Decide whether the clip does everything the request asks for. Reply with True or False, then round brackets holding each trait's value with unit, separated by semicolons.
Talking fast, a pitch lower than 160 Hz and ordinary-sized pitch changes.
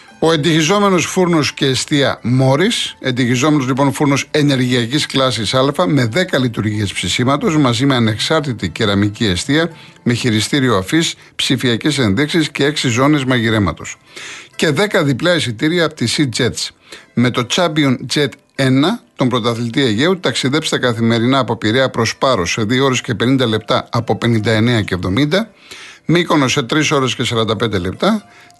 False (145 wpm; 135 Hz; 4.5 semitones)